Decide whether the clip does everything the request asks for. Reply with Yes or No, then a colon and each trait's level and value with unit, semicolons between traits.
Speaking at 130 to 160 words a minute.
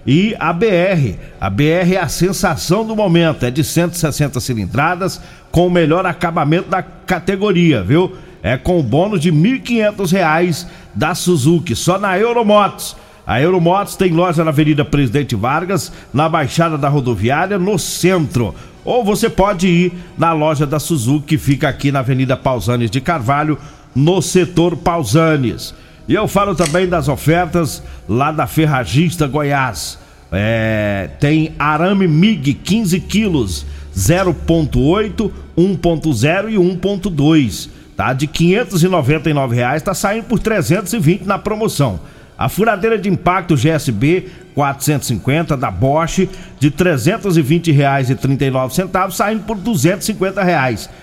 Yes: average, 135 wpm